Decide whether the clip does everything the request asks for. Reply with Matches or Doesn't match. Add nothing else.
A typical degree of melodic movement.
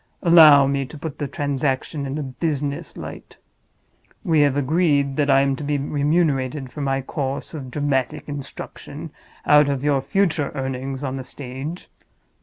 Doesn't match